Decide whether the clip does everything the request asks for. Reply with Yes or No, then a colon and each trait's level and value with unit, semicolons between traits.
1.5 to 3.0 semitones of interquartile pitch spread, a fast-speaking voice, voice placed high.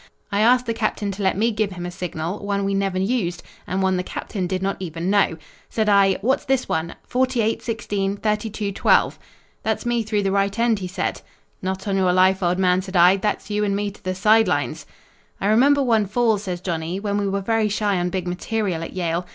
Yes: narrow, 2.6 semitones; fast, 225 wpm; high, 200 Hz